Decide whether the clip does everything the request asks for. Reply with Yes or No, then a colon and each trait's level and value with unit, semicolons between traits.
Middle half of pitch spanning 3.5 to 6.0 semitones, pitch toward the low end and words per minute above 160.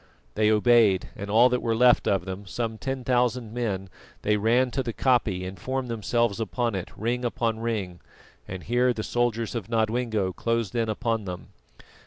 No: average, 3.0 semitones; low, 115 Hz; average, 180 wpm